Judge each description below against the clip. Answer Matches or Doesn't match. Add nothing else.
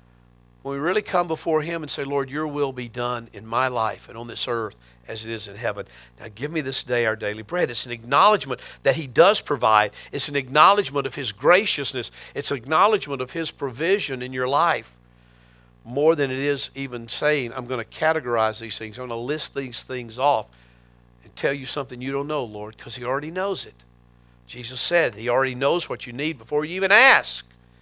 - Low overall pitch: Matches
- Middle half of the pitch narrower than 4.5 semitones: Doesn't match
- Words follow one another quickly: Matches